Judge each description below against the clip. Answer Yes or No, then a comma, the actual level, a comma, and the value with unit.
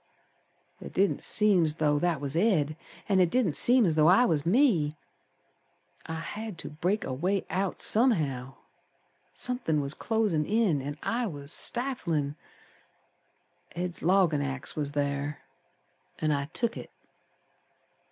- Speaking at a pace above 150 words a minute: No, average, 140 wpm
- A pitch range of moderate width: No, wide, 6.1 semitones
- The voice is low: No, medium, 165 Hz